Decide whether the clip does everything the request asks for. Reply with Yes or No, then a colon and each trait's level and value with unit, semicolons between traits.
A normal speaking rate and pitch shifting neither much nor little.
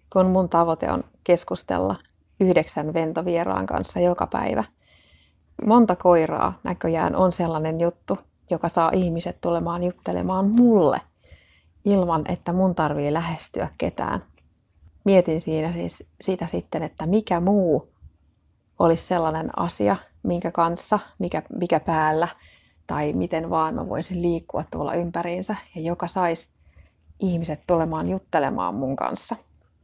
Yes: average, 120 wpm; average, 3.2 semitones